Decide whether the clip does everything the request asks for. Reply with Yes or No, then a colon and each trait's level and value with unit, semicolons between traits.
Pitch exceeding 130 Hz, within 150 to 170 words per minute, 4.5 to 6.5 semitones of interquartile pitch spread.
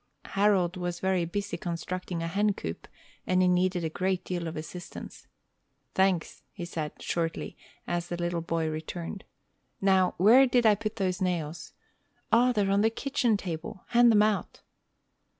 No: medium, 185 Hz; average, 160 wpm; average, 3.1 semitones